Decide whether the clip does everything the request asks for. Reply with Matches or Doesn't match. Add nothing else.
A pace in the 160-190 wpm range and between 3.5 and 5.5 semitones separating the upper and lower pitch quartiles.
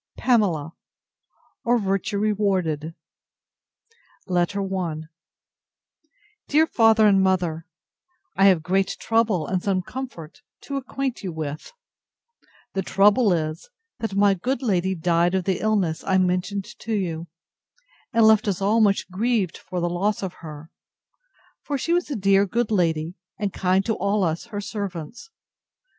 Doesn't match